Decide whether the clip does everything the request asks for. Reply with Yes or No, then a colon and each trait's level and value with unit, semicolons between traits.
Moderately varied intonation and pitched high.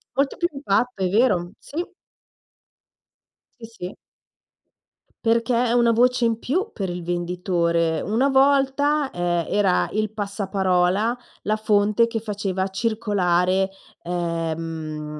Yes: average, 4.8 semitones; high, 205 Hz